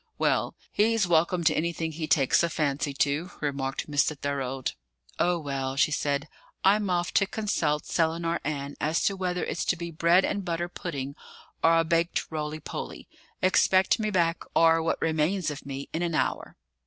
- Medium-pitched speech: Yes, medium, 165 Hz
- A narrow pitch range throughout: No, average, 3.3 semitones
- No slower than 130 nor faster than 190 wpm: Yes, average, 175 wpm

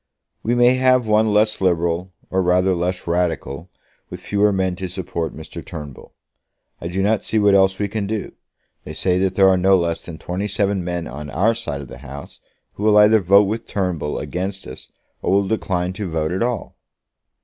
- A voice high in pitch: No, very low, 95 Hz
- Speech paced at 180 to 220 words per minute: Yes, average, 200 wpm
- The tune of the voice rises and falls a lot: No, average, 3.1 semitones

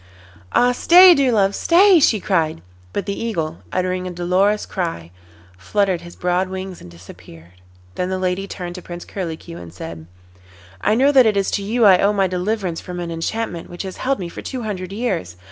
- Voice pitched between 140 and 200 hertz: Yes, medium, 185 Hz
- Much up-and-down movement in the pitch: No, average, 3.6 semitones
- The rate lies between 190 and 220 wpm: Yes, average, 195 wpm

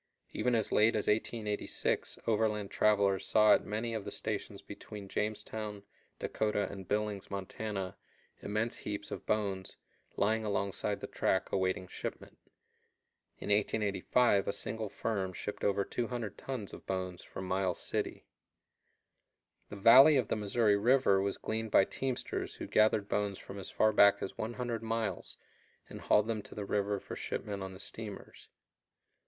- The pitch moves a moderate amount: No, narrow, 1.9 semitones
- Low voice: Yes, low, 105 Hz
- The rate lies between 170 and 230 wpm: No, average, 150 wpm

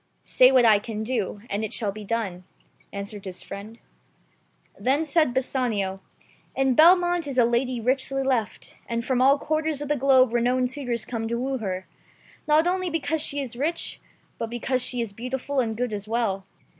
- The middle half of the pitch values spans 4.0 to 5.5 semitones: No, average, 3.6 semitones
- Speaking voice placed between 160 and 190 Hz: No, very high, 250 Hz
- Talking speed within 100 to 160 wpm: No, average, 180 wpm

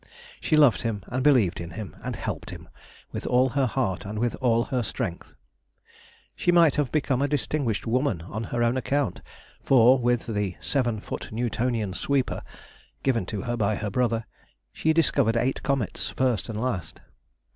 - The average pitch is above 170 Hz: No, low, 120 Hz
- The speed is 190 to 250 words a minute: No, average, 170 wpm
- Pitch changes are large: No, average, 3.6 semitones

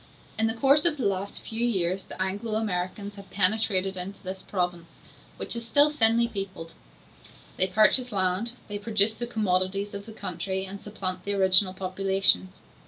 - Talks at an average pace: Yes, average, 170 wpm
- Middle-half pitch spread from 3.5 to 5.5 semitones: No, average, 3.0 semitones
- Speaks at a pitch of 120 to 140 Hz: No, high, 200 Hz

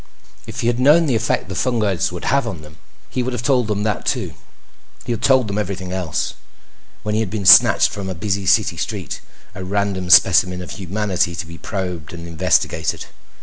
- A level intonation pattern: No, average, 3.8 semitones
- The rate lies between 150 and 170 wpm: No, average, 200 wpm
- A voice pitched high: No, low, 100 Hz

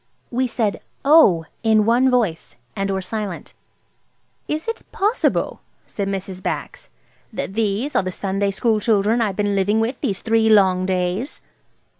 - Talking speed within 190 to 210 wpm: No, average, 150 wpm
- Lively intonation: No, average, 3.3 semitones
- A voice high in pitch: Yes, high, 210 Hz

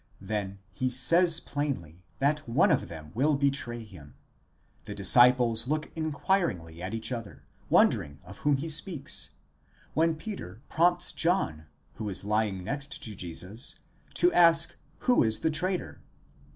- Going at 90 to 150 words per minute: Yes, average, 140 wpm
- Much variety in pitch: Yes, wide, 8.1 semitones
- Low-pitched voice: Yes, low, 125 Hz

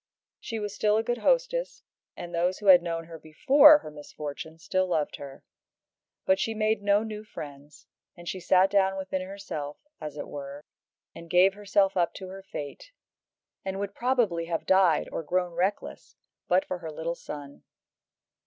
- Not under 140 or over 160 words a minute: No, average, 170 wpm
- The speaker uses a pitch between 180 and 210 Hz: Yes, medium, 185 Hz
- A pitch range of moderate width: Yes, average, 4.0 semitones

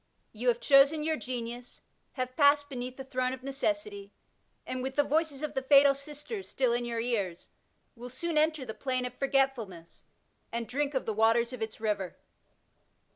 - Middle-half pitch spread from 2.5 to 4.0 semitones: Yes, average, 3.3 semitones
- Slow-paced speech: No, average, 180 wpm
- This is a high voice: Yes, very high, 260 Hz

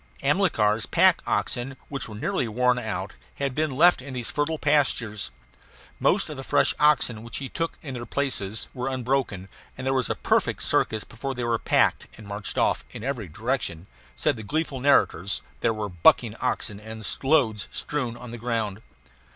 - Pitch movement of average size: Yes, average, 4.0 semitones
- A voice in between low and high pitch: No, low, 125 Hz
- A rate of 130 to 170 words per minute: No, average, 180 wpm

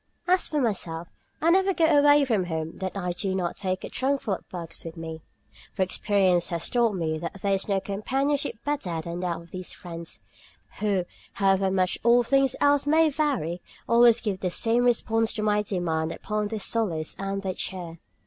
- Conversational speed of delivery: Yes, average, 190 wpm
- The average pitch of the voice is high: Yes, high, 195 Hz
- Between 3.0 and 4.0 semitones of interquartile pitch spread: No, wide, 5.5 semitones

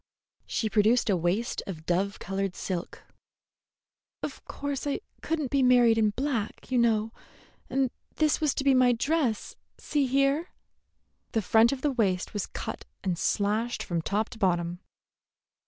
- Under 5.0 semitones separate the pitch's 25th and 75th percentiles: No, average, 5.3 semitones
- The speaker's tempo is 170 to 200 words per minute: No, average, 155 wpm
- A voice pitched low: No, high, 225 Hz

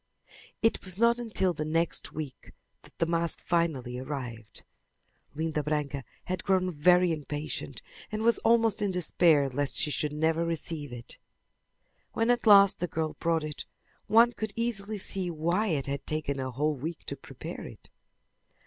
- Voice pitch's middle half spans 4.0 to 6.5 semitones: Yes, average, 4.7 semitones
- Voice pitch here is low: No, medium, 165 Hz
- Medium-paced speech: Yes, average, 160 wpm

